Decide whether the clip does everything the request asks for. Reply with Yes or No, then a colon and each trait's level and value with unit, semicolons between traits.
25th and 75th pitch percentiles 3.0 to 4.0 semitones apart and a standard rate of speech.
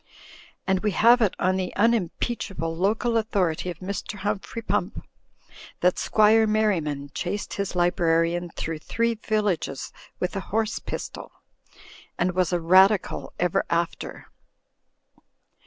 No: average, 3.7 semitones; slow, 125 wpm